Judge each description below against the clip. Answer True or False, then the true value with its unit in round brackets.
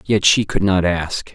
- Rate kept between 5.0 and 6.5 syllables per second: False (4.0 syllables/s)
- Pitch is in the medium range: False (95 Hz)